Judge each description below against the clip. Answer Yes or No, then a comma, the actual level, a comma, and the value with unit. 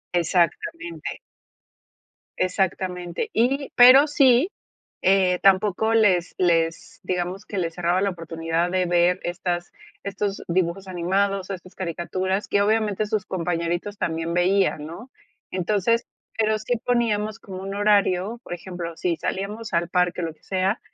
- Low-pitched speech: No, medium, 185 Hz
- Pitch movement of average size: Yes, average, 3.1 semitones